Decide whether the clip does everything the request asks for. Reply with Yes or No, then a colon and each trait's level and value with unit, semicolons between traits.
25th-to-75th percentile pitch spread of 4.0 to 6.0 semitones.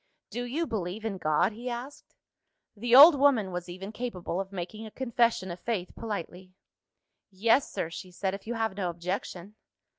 Yes: average, 4.5 semitones